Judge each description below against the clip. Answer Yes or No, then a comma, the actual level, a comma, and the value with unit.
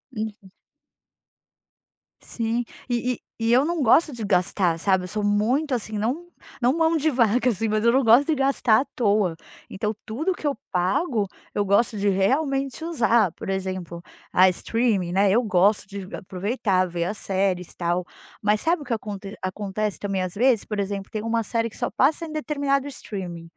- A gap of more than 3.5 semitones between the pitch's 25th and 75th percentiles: Yes, average, 4.7 semitones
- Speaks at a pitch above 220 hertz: No, high, 215 Hz